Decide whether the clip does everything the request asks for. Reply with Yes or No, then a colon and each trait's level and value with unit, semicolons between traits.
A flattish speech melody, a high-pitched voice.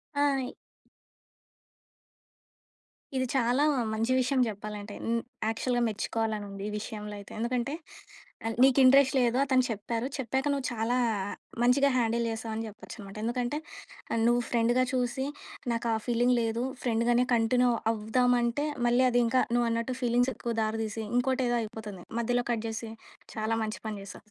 Yes: narrow, 2.1 semitones; high, 235 Hz